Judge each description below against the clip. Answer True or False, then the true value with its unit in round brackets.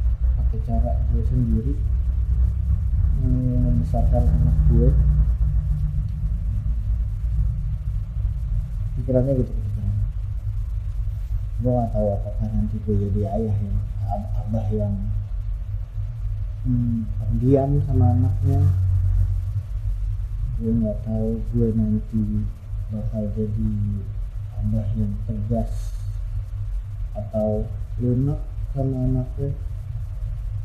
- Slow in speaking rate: True (75 wpm)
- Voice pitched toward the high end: False (105 Hz)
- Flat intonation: True (1.9 semitones)